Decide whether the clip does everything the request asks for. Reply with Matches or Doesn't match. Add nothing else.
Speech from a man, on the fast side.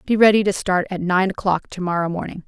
Doesn't match